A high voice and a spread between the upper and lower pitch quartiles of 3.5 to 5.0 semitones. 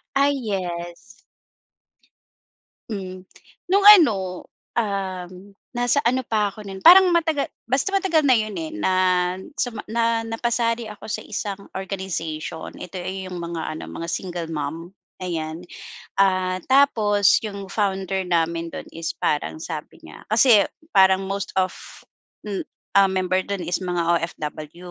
Yes: high, 195 Hz; average, 4.5 semitones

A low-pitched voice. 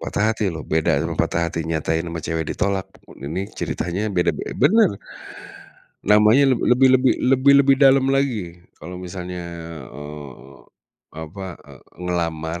Yes: very low, 90 Hz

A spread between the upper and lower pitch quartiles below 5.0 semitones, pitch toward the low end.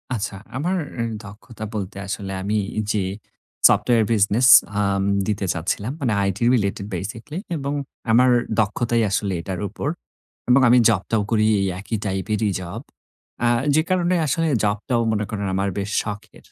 Yes: average, 3.2 semitones; low, 105 Hz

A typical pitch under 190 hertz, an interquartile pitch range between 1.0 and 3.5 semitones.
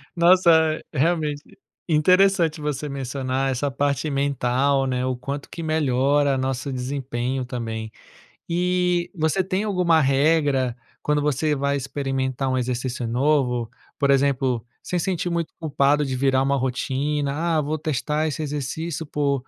Yes: medium, 140 Hz; average, 3.2 semitones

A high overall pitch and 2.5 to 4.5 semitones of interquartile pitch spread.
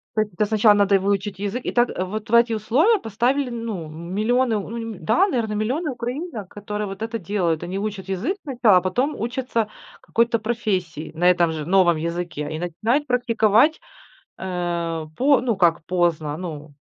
No: high, 210 Hz; average, 5.0 semitones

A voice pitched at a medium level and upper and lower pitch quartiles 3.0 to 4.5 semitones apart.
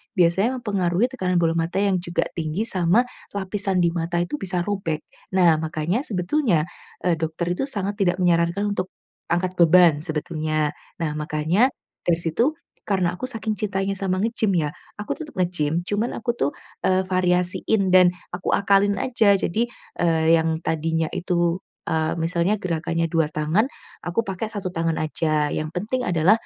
Yes: medium, 180 Hz; average, 3.4 semitones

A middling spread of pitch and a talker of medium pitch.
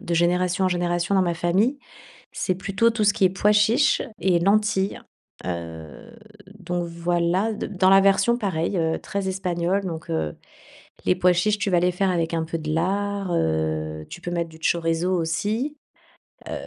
Yes: average, 3.0 semitones; medium, 180 Hz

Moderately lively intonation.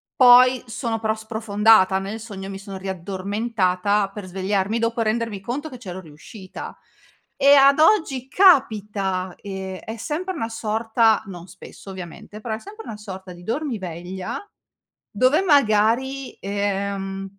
Yes: average, 3.8 semitones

